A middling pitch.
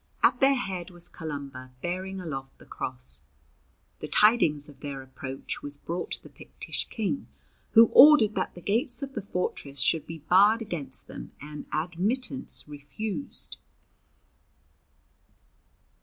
Yes: medium, 175 Hz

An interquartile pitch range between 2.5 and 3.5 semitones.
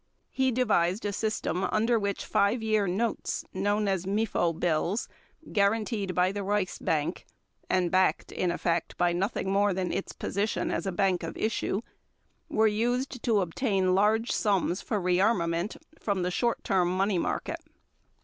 Yes: average, 3.1 semitones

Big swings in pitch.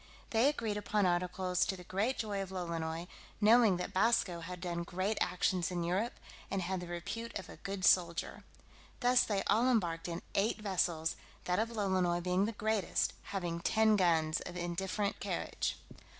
No: average, 3.4 semitones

